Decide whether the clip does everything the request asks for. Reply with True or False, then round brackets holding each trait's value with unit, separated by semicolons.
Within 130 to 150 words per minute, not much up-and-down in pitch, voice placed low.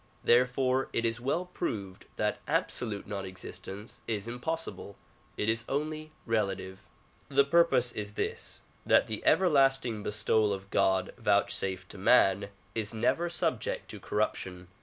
False (140 wpm; 5.2 semitones; 110 Hz)